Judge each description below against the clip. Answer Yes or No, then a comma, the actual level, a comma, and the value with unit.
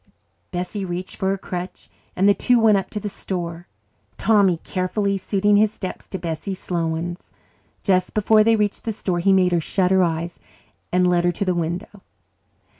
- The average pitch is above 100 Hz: Yes, medium, 185 Hz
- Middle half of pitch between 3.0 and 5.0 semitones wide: No, narrow, 2.5 semitones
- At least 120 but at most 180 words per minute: No, average, 190 wpm